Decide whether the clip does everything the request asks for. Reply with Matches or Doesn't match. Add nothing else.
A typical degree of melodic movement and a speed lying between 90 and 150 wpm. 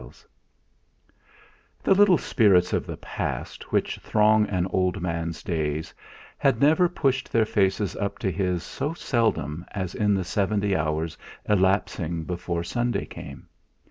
Matches